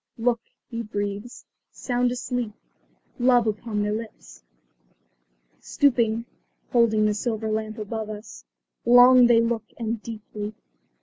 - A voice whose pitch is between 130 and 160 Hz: No, high, 225 Hz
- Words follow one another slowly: Yes, slow, 115 wpm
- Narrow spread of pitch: Yes, narrow, 2.2 semitones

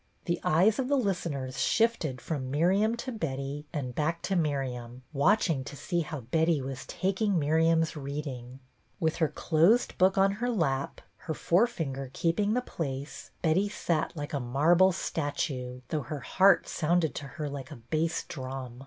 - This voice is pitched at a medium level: Yes, medium, 155 Hz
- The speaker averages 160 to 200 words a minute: Yes, average, 165 wpm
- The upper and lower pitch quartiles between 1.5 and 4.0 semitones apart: No, average, 5.2 semitones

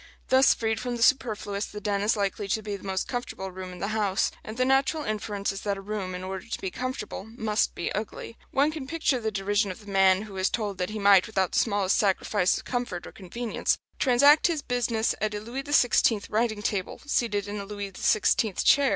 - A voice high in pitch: Yes, high, 210 Hz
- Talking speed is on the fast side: Yes, fast, 225 wpm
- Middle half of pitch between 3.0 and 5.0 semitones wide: Yes, average, 3.5 semitones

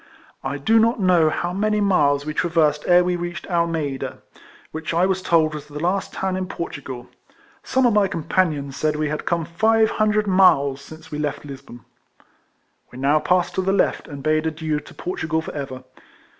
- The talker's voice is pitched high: No, medium, 160 Hz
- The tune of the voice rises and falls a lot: No, average, 4.0 semitones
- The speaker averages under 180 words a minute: No, average, 185 wpm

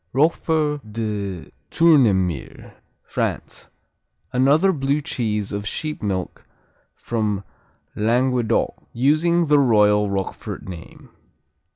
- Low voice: Yes, low, 120 Hz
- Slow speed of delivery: Yes, slow, 85 wpm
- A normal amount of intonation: No, wide, 6.2 semitones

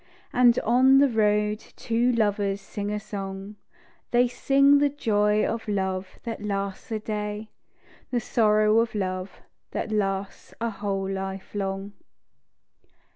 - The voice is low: No, high, 210 Hz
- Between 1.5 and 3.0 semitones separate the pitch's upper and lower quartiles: Yes, average, 2.7 semitones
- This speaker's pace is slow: Yes, slow, 130 wpm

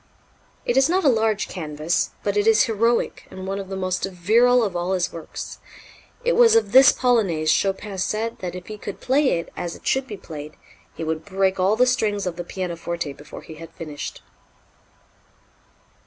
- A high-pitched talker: Yes, high, 195 Hz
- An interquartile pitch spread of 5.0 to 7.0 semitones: Yes, wide, 5.5 semitones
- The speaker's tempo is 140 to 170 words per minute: No, average, 190 wpm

